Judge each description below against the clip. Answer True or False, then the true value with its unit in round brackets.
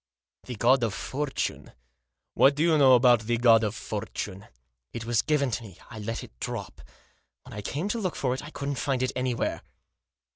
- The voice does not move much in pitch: False (3.9 semitones)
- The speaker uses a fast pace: True (210 wpm)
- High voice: False (125 Hz)